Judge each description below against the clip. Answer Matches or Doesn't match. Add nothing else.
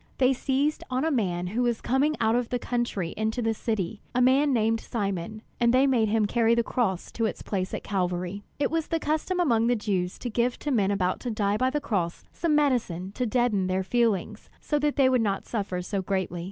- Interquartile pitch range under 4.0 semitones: Doesn't match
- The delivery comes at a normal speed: Doesn't match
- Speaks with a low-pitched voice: Doesn't match